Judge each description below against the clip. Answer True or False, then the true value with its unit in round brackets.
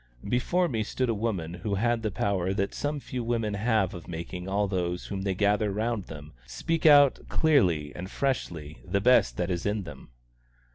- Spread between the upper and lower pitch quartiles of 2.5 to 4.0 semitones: False (5.0 semitones)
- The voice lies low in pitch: True (100 Hz)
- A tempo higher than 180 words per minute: True (190 wpm)